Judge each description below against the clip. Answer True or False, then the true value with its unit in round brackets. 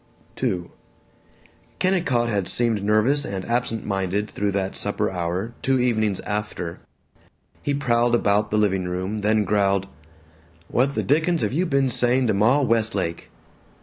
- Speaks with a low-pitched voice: True (110 Hz)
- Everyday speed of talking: True (145 wpm)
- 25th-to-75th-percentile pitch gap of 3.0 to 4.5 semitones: True (4.0 semitones)